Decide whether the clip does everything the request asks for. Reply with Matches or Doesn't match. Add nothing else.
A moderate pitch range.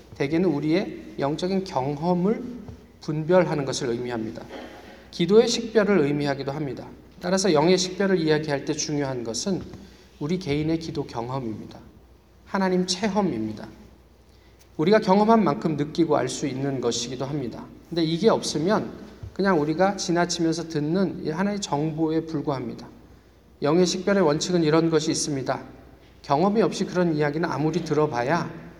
Matches